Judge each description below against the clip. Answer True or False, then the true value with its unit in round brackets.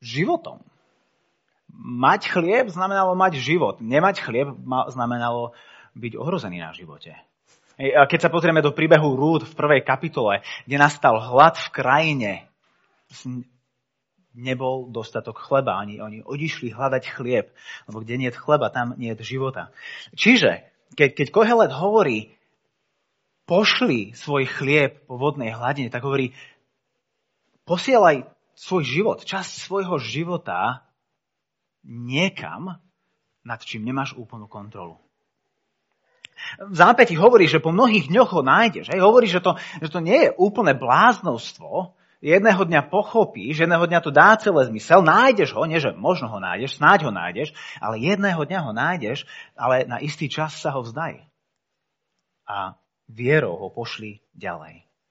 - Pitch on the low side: False (145 Hz)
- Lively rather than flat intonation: True (6.6 semitones)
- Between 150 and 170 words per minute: False (135 wpm)